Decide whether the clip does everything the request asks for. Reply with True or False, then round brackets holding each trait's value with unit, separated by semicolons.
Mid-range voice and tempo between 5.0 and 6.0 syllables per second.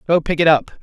False (160 Hz; 6.3 syllables/s)